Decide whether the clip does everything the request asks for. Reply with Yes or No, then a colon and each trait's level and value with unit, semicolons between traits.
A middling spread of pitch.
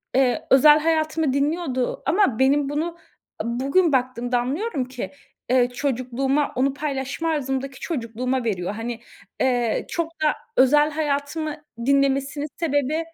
Yes: average, 3.1 semitones